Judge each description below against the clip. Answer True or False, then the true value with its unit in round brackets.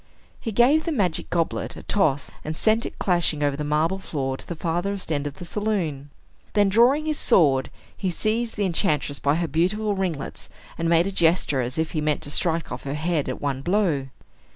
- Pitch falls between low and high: True (170 Hz)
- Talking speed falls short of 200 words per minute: False (205 wpm)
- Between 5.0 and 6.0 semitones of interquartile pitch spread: True (5.3 semitones)